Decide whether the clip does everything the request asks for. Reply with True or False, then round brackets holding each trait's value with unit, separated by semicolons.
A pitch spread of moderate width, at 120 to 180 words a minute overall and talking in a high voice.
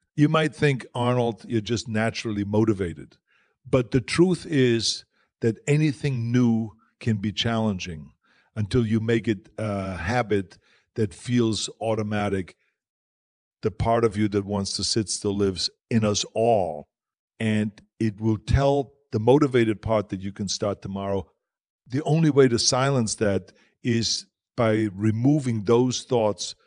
False (3.1 semitones; 140 wpm; 110 Hz)